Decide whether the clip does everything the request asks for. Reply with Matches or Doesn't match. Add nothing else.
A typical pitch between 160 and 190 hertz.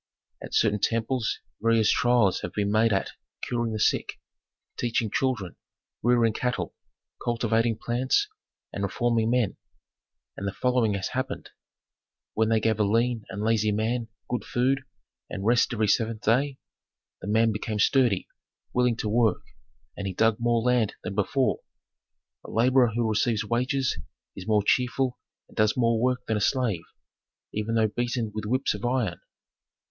Doesn't match